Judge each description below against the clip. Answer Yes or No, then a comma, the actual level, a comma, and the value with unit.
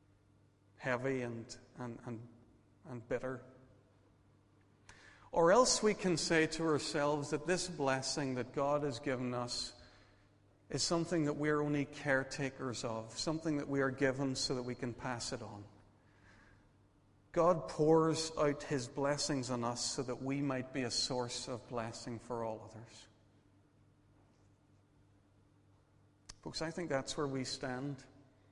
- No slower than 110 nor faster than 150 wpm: Yes, average, 140 wpm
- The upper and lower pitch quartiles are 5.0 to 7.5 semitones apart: Yes, wide, 5.5 semitones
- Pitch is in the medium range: No, low, 125 Hz